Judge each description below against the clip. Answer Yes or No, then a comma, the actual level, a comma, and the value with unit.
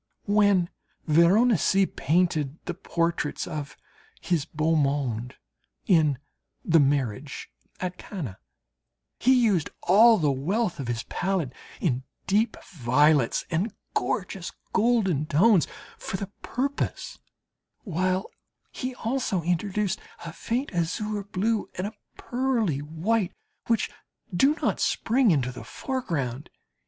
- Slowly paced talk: Yes, slow, 115 wpm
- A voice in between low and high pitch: Yes, medium, 180 Hz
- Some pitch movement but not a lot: No, wide, 6.1 semitones